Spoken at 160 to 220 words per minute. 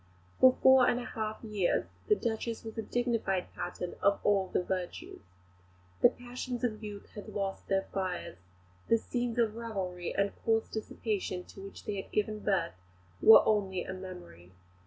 Yes: average, 165 wpm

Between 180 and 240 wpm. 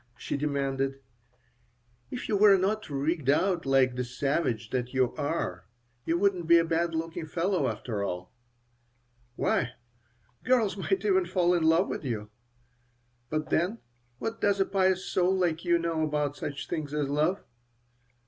No: average, 155 wpm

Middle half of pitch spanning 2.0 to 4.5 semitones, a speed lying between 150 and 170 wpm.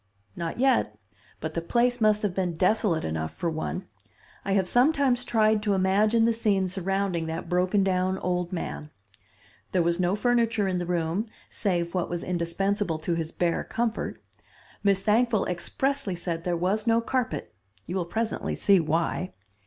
Yes: average, 4.1 semitones; average, 165 wpm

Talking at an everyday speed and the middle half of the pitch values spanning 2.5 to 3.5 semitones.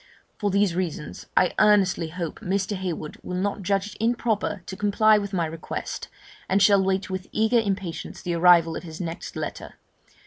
Yes: average, 175 wpm; average, 2.9 semitones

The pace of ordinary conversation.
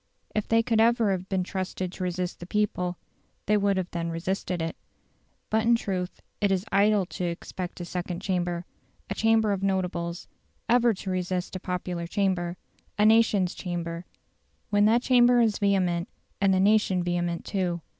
Yes: average, 170 wpm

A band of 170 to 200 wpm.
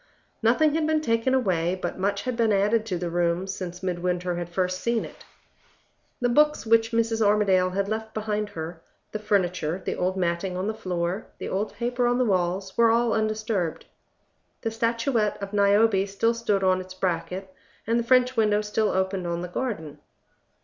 Yes: average, 185 wpm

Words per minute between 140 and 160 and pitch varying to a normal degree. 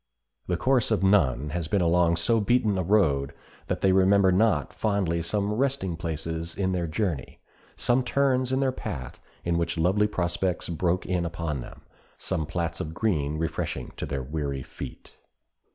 No: average, 170 wpm; average, 4.1 semitones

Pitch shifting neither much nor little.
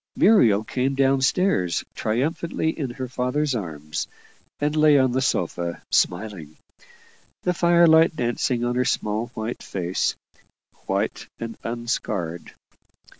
No: wide, 6.0 semitones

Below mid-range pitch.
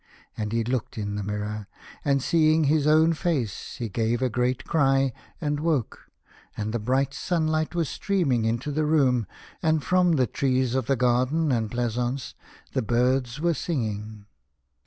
Yes: low, 130 Hz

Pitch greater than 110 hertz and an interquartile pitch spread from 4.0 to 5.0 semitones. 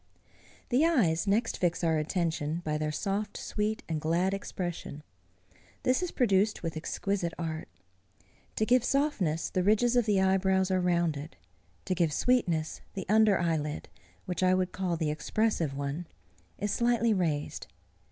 Yes: medium, 185 Hz; average, 4.7 semitones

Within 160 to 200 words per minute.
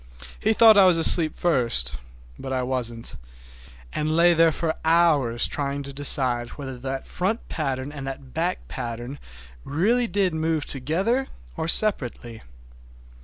No: slow, 135 wpm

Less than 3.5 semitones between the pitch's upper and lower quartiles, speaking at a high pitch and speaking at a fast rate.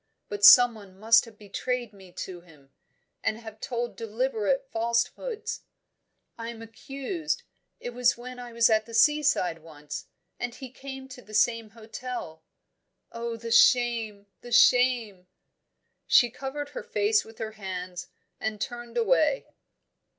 No: average, 2.8 semitones; high, 230 Hz; average, 140 wpm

